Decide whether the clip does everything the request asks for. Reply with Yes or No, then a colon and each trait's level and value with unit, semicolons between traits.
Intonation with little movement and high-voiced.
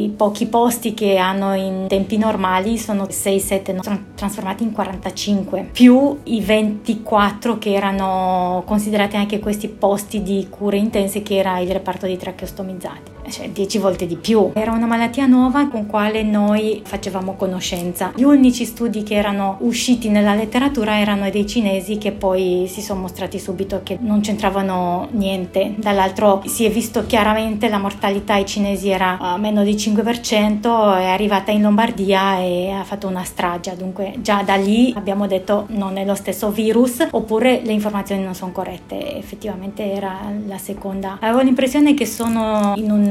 Yes: narrow, 2.1 semitones; high, 205 Hz